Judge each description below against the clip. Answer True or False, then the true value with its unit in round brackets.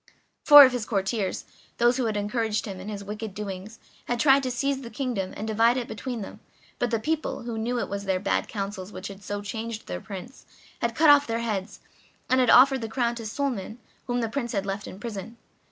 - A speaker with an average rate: False (225 wpm)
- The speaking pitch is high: True (225 Hz)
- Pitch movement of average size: True (3.3 semitones)